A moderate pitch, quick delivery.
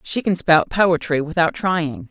No: medium, 165 Hz; average, 170 wpm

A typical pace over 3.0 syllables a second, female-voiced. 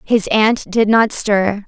Yes: 3.3 syllables/s; female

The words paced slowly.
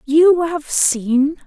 Yes: slow, 125 wpm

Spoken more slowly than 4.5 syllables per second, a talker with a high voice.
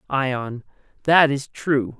No: 2.9 syllables/s; low, 135 Hz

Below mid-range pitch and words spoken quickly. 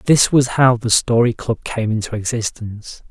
No: low, 115 Hz; average, 175 wpm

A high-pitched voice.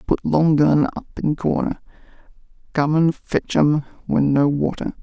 No: medium, 150 Hz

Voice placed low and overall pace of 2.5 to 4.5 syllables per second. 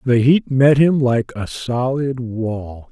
Yes: low, 125 Hz; 3.2 syllables/s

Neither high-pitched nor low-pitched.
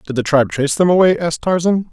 Yes: medium, 160 Hz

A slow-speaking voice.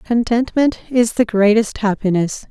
Yes: slow, 120 wpm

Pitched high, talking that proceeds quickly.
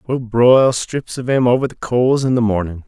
No: low, 120 Hz; fast, 230 wpm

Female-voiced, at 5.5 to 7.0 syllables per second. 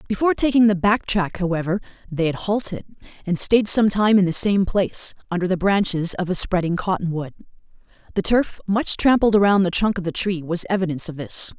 Yes: female; 5.7 syllables/s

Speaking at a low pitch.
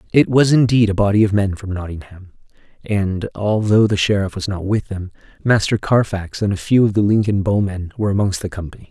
Yes: low, 100 Hz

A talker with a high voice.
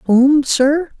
Yes: very high, 280 Hz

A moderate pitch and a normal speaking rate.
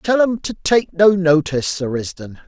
Yes: medium, 175 Hz; average, 195 wpm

